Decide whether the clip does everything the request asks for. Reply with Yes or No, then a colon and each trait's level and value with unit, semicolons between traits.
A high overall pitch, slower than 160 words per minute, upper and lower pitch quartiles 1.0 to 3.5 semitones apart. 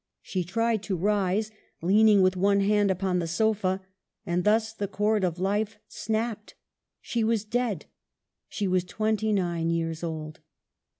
Yes: high, 200 Hz; average, 145 wpm; average, 3.1 semitones